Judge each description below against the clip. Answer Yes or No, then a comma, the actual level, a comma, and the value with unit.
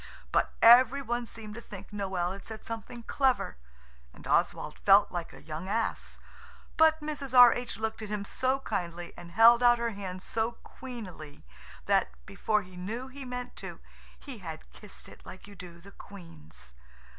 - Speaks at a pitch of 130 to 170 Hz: No, high, 215 Hz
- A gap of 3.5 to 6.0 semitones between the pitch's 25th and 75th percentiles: Yes, average, 4.9 semitones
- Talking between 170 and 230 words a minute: Yes, average, 175 wpm